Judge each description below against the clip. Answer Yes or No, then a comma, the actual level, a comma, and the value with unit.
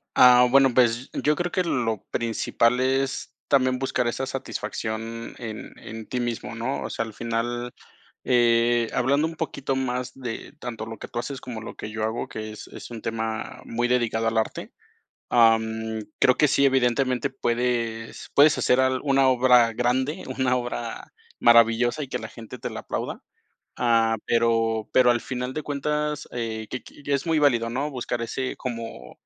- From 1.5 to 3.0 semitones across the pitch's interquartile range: Yes, narrow, 2.4 semitones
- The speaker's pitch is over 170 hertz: No, low, 120 Hz